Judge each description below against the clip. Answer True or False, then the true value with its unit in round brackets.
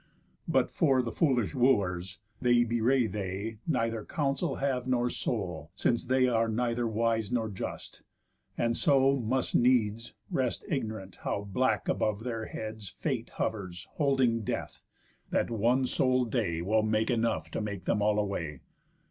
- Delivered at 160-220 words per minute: False (150 wpm)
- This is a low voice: True (115 Hz)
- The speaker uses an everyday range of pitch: True (3.2 semitones)